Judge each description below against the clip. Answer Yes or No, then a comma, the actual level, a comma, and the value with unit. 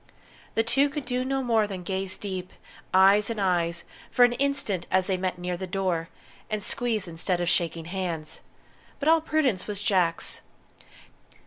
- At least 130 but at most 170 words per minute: Yes, average, 165 wpm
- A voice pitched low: No, high, 190 Hz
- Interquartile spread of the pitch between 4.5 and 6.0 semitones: Yes, average, 5.1 semitones